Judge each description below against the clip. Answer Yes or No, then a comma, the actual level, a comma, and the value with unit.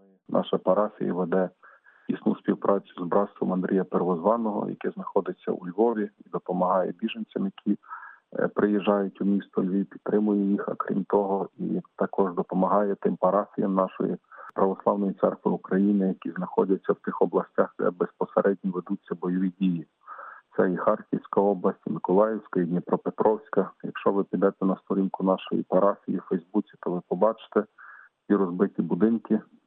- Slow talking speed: No, average, 140 wpm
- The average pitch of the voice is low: Yes, very low, 95 Hz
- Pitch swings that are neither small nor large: No, narrow, 1.5 semitones